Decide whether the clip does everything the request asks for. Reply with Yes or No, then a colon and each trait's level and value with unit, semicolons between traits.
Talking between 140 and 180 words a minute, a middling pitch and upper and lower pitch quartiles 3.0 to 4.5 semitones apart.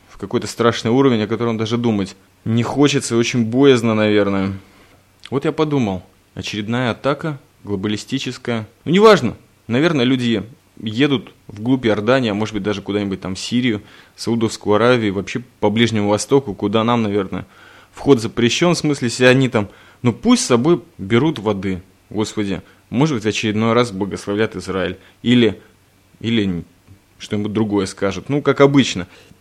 No: average, 150 wpm; low, 110 Hz; average, 4.1 semitones